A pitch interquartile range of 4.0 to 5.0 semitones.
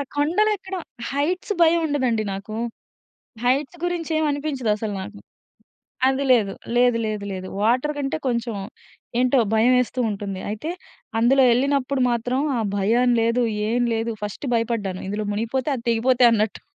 Yes: average, 4.4 semitones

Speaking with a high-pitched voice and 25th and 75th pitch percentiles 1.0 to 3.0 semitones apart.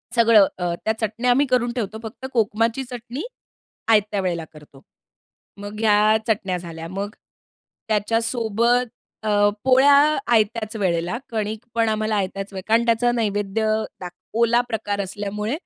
Yes: high, 215 Hz; narrow, 2.6 semitones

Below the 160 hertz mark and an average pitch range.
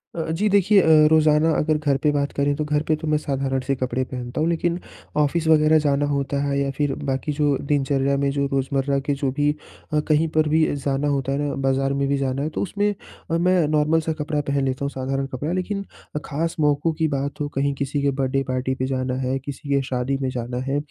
No: medium, 140 Hz; narrow, 2.1 semitones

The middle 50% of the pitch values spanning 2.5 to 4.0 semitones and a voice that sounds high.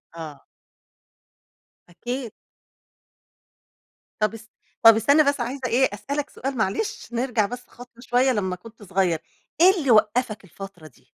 No: average, 4.4 semitones; high, 230 Hz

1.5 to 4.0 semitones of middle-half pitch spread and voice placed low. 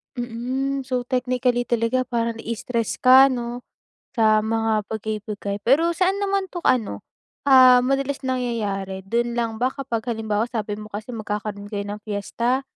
No: average, 3.0 semitones; high, 235 Hz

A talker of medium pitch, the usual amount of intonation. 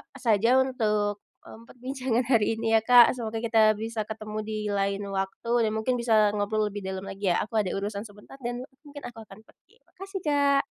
No: high, 220 Hz; average, 3.0 semitones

